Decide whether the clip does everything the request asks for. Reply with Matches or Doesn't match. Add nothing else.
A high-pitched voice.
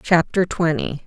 Doesn't match